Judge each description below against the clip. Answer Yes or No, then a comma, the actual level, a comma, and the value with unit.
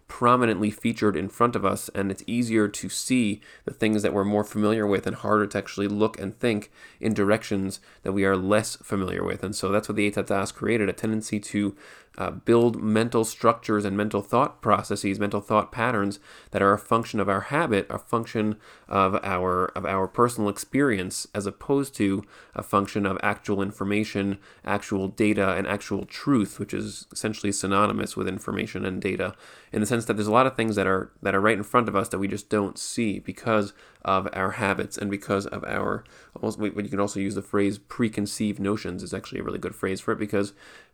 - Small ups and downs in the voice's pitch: Yes, narrow, 1.7 semitones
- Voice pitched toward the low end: Yes, low, 105 Hz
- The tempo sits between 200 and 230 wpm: Yes, fast, 205 wpm